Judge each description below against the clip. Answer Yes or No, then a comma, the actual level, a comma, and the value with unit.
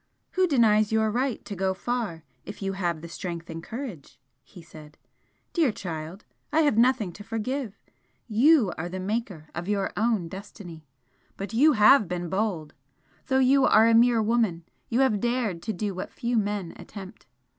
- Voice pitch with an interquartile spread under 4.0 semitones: No, average, 5.1 semitones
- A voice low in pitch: No, high, 210 Hz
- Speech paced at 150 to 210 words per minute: Yes, average, 175 wpm